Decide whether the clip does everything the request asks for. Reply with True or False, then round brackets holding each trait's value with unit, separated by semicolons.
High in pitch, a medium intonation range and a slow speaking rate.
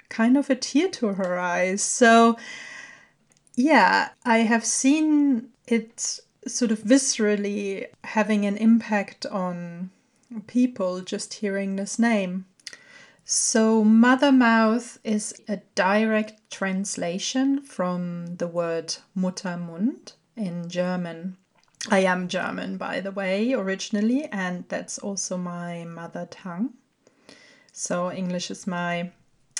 True (210 Hz; 4.6 semitones; 110 wpm)